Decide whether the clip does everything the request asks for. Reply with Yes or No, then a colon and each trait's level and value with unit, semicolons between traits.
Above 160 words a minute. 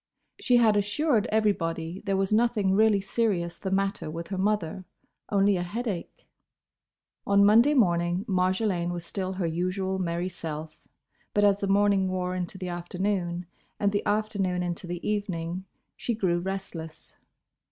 No: average, 150 wpm